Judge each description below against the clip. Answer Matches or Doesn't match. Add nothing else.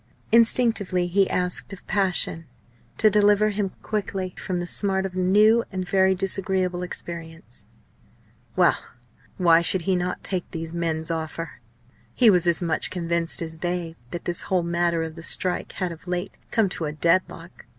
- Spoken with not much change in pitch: Matches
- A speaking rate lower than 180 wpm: Matches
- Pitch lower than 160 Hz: Doesn't match